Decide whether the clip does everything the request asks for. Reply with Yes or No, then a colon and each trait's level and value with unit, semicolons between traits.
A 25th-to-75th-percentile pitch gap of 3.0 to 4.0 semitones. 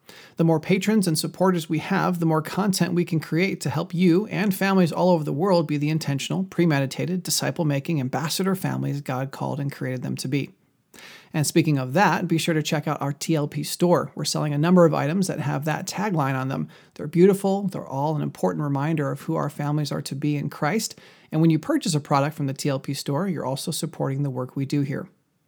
Yes: average, 3.4 semitones